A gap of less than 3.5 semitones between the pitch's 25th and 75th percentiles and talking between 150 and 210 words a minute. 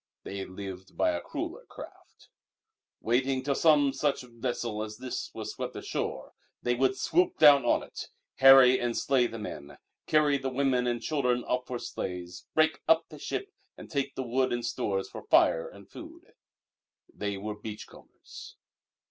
No: average, 4.3 semitones; average, 165 wpm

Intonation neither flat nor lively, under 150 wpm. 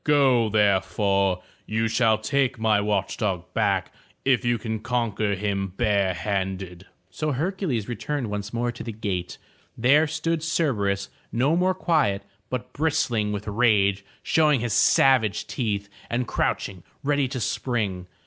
Yes: average, 4.7 semitones; average, 140 wpm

